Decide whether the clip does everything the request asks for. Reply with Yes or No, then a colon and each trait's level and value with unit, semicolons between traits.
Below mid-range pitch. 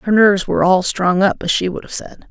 No: high, 190 Hz